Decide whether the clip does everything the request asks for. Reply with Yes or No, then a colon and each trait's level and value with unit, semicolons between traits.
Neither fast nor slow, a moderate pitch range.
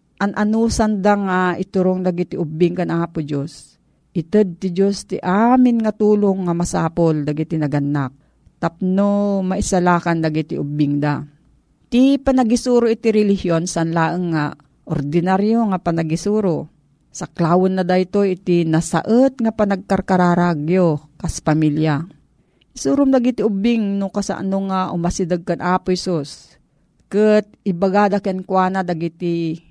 Yes: average, 120 wpm; average, 3.6 semitones